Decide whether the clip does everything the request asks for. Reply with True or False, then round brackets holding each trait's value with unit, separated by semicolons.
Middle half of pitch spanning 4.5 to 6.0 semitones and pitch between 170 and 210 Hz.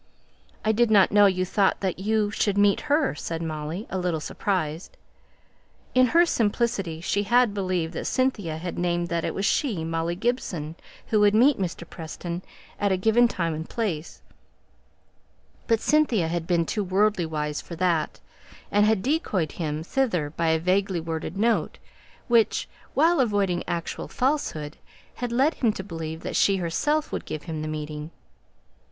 True (5.1 semitones; 185 Hz)